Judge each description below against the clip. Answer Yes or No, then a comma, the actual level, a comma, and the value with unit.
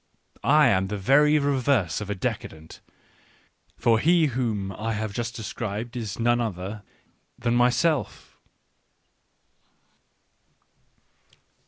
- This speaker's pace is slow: Yes, slow, 105 wpm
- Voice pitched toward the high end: No, low, 115 Hz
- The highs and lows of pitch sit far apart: No, average, 4.3 semitones